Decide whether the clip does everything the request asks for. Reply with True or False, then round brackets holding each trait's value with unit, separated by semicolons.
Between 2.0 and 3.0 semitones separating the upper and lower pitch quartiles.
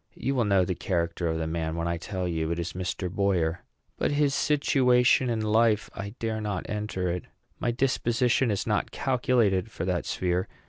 False (5.2 semitones)